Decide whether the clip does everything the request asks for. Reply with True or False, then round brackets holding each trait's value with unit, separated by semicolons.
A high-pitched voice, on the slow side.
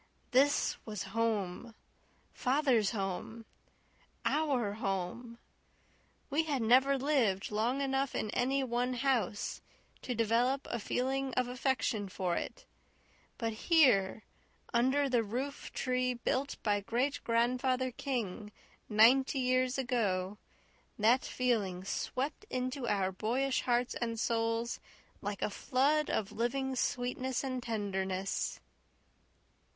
True (245 Hz; 115 wpm)